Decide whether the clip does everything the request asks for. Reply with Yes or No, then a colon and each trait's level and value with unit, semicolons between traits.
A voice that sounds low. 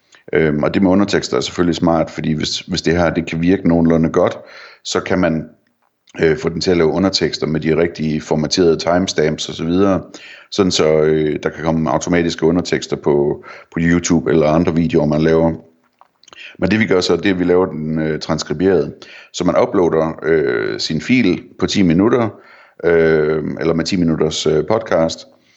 Yes: very low, 80 Hz